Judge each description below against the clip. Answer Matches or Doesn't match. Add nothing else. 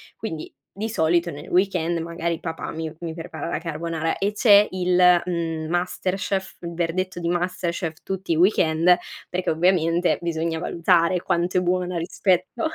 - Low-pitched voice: Doesn't match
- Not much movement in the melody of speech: Matches